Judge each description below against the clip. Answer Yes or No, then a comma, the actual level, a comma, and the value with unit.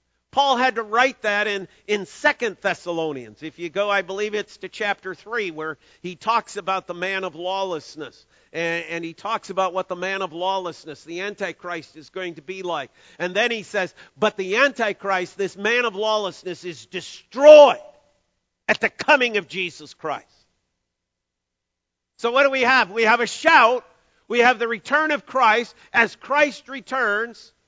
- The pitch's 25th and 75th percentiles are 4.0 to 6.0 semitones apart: Yes, average, 4.8 semitones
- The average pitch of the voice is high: Yes, high, 195 Hz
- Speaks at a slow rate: No, average, 175 wpm